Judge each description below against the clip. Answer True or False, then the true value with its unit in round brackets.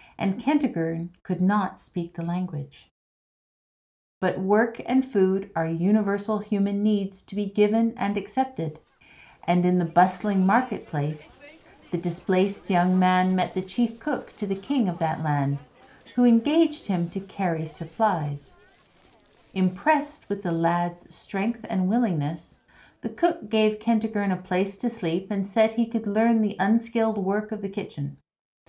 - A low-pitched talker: False (195 Hz)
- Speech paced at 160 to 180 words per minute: False (150 wpm)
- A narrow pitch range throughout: False (4.1 semitones)